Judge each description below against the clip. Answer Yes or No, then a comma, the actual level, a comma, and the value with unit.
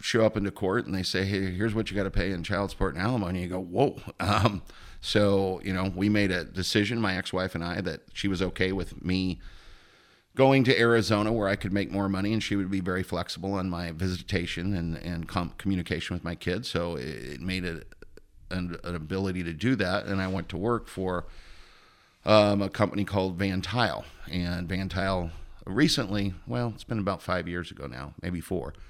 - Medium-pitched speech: No, very low, 95 Hz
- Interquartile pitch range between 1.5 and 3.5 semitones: Yes, narrow, 2.4 semitones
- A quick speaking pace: Yes, fast, 215 wpm